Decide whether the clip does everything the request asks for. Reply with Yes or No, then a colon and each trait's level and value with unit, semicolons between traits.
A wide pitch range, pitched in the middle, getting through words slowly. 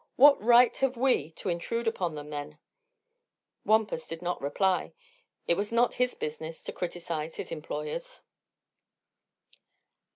Yes: wide, 7.1 semitones; medium, 180 Hz; slow, 130 wpm